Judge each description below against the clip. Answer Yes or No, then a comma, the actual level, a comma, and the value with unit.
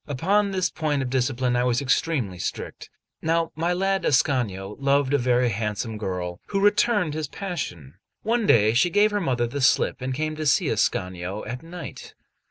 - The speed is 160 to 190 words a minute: Yes, average, 180 wpm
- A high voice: No, low, 135 Hz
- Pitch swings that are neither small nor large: No, wide, 6.4 semitones